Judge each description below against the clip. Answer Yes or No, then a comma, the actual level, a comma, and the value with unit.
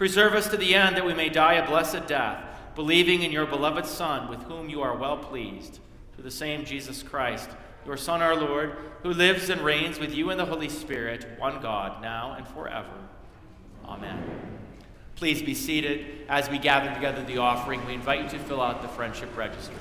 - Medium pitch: Yes, medium, 150 Hz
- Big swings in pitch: No, average, 3.3 semitones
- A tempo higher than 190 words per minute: Yes, average, 200 wpm